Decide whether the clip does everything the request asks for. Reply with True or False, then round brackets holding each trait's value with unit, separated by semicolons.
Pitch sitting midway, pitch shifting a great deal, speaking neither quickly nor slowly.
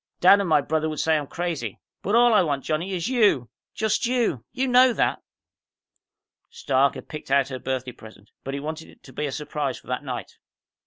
False (155 Hz; 6.5 semitones; 210 wpm)